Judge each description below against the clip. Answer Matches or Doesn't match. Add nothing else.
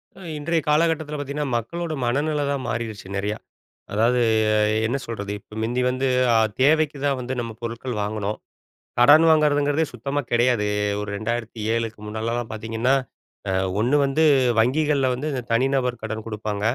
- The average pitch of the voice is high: Doesn't match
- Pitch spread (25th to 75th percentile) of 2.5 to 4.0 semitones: Doesn't match